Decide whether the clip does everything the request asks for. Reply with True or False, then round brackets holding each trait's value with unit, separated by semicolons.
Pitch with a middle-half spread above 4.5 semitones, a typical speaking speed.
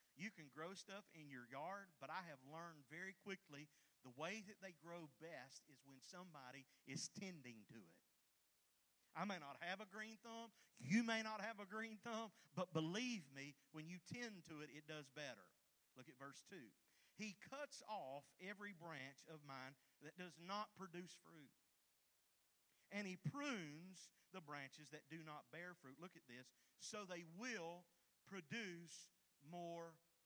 True (4.9 semitones; 170 wpm)